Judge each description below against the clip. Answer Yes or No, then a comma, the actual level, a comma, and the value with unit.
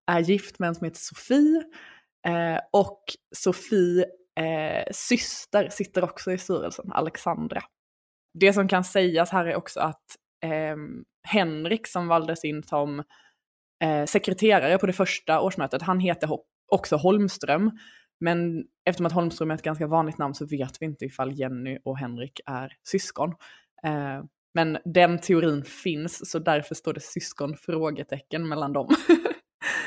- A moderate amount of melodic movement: Yes, average, 3.9 semitones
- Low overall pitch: No, medium, 170 Hz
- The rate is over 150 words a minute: No, average, 145 wpm